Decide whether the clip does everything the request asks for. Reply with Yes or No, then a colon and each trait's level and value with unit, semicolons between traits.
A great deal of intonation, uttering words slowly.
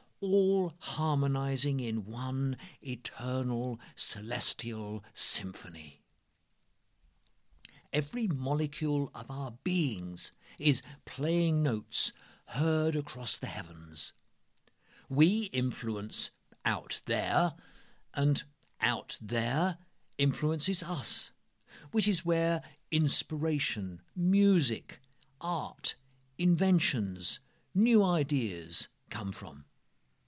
Yes: wide, 5.7 semitones; slow, 75 wpm